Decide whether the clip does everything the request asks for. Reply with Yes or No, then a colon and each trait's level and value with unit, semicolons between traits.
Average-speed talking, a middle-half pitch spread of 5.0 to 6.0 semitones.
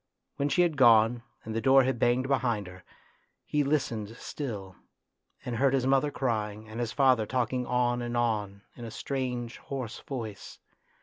No: average, 170 wpm; average, 3.2 semitones